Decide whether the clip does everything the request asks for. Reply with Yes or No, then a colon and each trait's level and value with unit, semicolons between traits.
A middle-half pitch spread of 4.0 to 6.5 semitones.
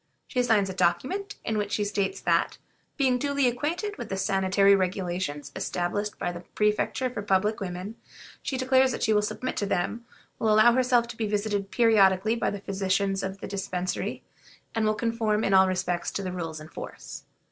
No: average, 3.5 semitones